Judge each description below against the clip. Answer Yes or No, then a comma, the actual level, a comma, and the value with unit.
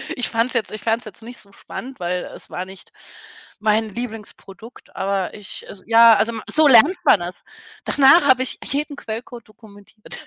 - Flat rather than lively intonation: No, average, 3.6 semitones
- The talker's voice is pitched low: No, high, 225 Hz